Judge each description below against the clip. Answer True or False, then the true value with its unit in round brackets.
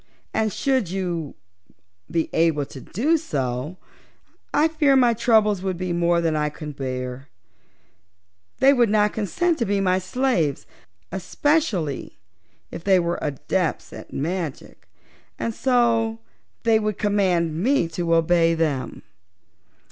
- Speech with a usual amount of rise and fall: False (5.8 semitones)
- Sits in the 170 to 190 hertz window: True (185 Hz)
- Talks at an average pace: False (130 wpm)